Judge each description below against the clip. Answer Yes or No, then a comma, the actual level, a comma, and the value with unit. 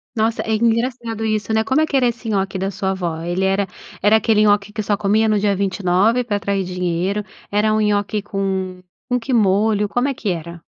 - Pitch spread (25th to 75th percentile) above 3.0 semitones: No, narrow, 2.5 semitones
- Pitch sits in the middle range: No, high, 205 Hz